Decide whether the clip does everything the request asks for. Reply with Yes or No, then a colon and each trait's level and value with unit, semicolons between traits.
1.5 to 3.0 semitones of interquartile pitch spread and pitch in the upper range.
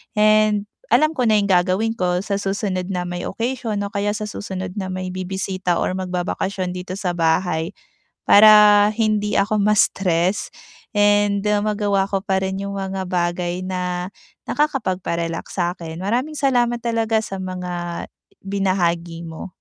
Yes: narrow, 2.6 semitones; high, 195 Hz